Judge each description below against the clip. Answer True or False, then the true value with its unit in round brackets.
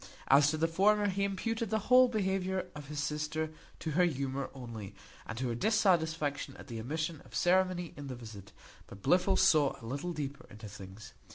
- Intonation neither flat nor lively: False (6.0 semitones)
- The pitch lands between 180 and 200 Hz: False (155 Hz)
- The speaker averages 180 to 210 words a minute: True (190 wpm)